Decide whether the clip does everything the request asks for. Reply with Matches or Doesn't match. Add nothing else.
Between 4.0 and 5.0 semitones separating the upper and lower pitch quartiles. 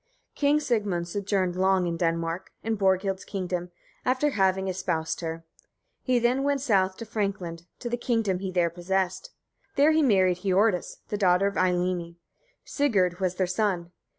Doesn't match